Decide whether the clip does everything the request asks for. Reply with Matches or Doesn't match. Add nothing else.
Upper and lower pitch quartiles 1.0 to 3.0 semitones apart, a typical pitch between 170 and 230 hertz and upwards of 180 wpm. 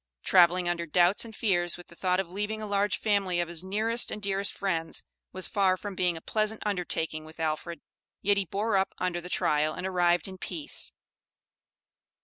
Matches